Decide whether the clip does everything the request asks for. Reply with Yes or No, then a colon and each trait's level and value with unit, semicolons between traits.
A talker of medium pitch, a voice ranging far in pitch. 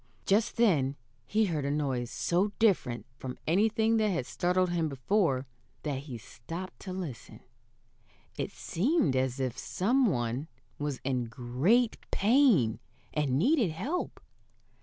Yes: medium, 165 Hz; wide, 8.2 semitones